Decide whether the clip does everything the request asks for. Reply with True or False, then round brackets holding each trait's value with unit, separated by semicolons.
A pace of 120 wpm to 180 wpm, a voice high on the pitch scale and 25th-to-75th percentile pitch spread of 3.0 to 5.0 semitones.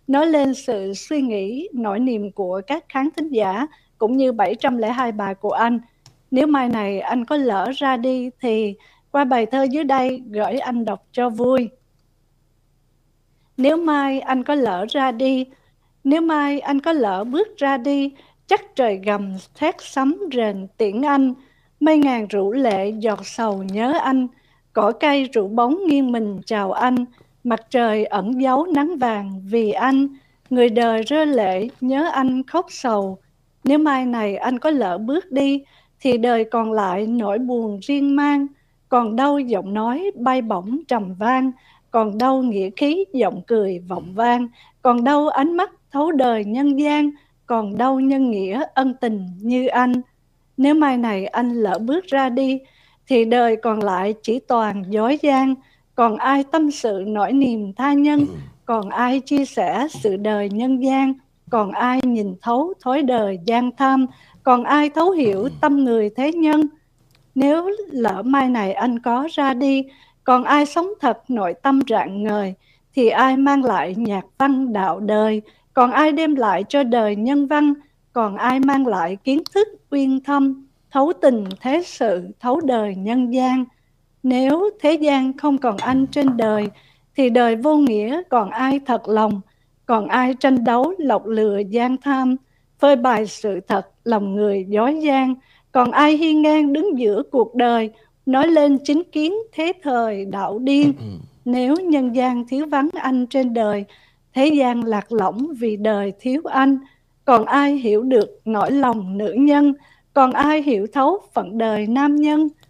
True (170 wpm; 255 Hz; 4.4 semitones)